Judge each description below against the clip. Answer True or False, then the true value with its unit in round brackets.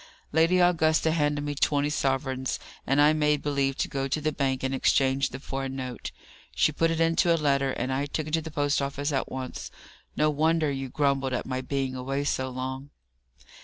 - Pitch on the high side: False (140 Hz)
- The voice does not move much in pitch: True (2.3 semitones)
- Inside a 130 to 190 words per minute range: False (205 wpm)